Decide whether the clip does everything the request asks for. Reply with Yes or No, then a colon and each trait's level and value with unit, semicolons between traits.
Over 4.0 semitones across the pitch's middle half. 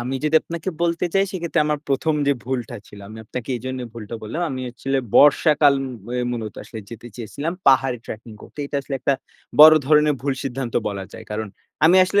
Yes: average, 4.5 semitones